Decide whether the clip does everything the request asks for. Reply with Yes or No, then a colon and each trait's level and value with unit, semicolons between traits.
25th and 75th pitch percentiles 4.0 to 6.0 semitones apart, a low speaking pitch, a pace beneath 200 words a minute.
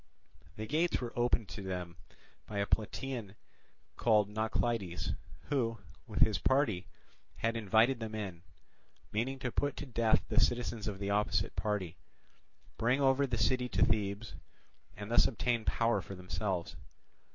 No: average, 3.3 semitones; low, 110 Hz; average, 145 wpm